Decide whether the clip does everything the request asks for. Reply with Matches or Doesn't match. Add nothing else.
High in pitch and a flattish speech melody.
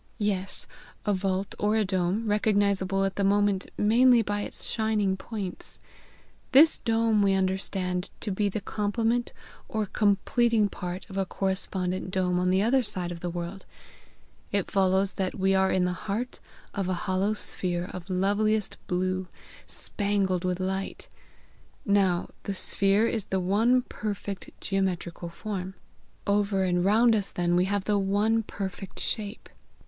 Matches